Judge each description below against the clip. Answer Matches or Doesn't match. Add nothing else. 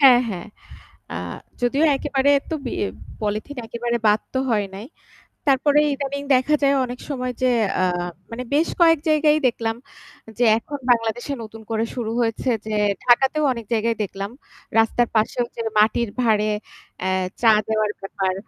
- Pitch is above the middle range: Matches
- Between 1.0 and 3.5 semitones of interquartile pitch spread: Doesn't match